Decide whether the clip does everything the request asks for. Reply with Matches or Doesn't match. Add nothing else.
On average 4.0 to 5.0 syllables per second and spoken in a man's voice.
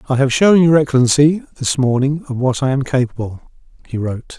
Doesn't match